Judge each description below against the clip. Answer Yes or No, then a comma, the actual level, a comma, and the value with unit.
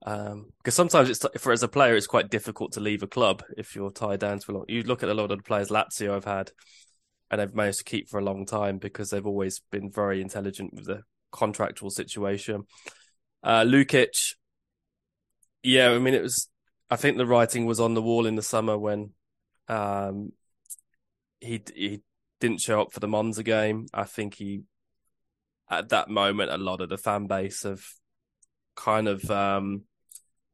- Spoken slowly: No, average, 190 wpm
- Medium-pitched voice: No, low, 105 Hz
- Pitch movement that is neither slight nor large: No, narrow, 1.8 semitones